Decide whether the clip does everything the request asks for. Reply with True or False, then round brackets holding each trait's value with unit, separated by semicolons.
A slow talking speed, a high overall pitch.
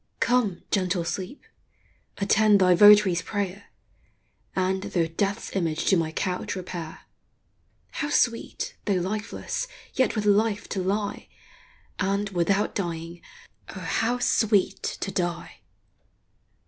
True (115 wpm; 195 Hz)